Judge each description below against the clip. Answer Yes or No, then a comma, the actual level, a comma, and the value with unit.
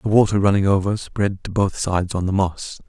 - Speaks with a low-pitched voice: Yes, very low, 95 Hz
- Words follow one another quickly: Yes, fast, 230 wpm